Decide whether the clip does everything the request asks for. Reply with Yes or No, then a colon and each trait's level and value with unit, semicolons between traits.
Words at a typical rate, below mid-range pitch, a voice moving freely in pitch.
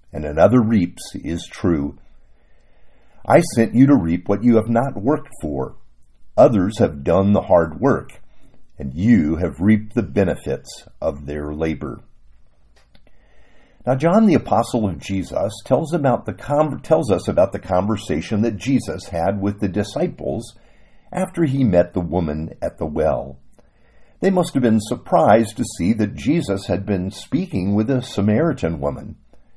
Yes: average, 155 wpm; low, 105 Hz; wide, 5.9 semitones